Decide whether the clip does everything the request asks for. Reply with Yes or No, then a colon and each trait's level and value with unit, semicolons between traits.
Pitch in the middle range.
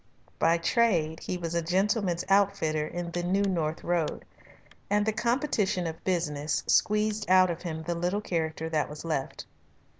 Yes: medium, 175 Hz